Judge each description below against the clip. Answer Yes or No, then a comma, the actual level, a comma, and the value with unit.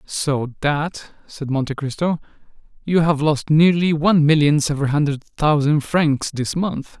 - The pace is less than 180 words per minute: Yes, average, 145 wpm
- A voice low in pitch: No, medium, 150 Hz